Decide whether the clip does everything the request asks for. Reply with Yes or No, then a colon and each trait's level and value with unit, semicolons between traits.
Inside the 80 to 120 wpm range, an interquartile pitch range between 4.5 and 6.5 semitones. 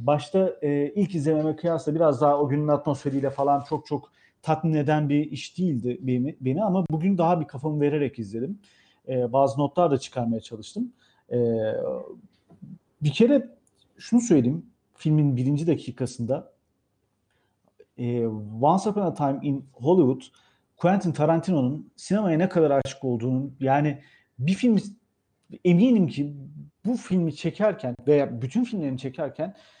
No: average, 135 wpm; average, 4.9 semitones